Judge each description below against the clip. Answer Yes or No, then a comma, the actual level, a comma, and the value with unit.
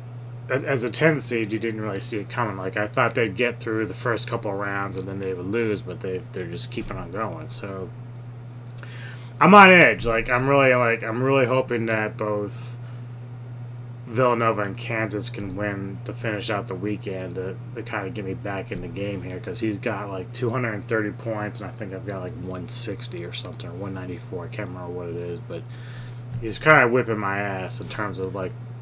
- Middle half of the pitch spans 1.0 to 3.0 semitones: Yes, narrow, 2.4 semitones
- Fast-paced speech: Yes, fast, 210 wpm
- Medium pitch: No, low, 115 Hz